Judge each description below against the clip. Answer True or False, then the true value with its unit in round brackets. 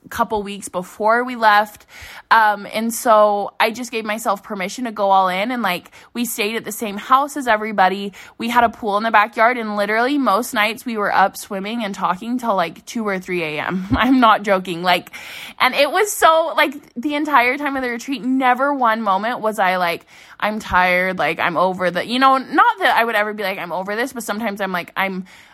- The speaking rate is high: True (220 wpm)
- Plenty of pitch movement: False (3.9 semitones)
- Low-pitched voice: False (215 Hz)